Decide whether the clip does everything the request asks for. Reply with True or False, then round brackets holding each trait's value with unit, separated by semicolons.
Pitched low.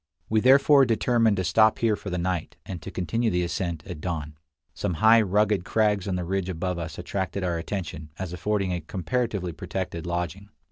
True (95 Hz)